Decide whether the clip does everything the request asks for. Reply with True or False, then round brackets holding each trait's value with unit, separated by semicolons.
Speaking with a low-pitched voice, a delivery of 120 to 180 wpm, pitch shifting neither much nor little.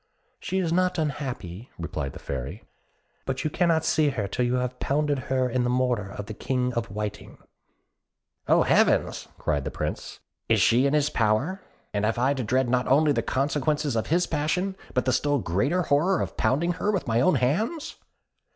False (130 Hz; 195 wpm; 4.6 semitones)